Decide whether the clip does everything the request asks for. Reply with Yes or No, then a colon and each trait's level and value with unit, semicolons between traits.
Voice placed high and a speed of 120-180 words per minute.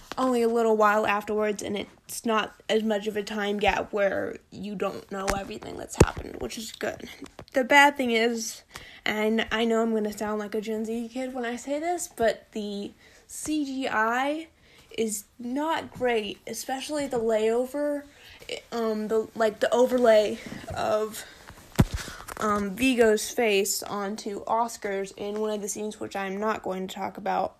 Yes: high, 220 Hz; average, 165 wpm